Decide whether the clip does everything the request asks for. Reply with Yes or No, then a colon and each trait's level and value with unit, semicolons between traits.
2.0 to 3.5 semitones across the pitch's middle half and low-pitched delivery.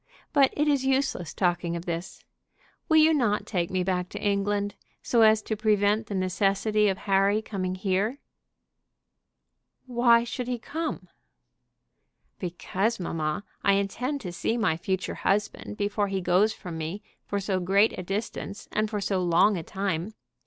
No: average, 3.0 semitones; high, 200 Hz